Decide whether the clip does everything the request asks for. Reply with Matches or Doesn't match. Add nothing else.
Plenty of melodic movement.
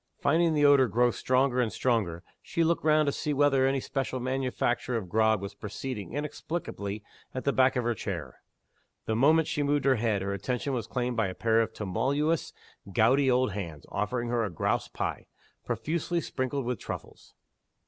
Doesn't match